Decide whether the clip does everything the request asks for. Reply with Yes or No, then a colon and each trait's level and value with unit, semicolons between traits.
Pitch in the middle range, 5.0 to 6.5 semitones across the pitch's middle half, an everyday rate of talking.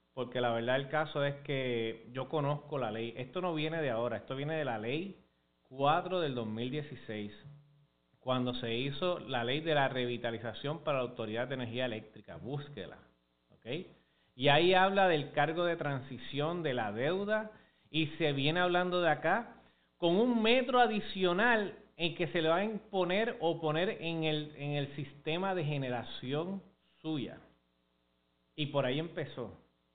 Yes: medium, 145 Hz; wide, 5.5 semitones; average, 160 wpm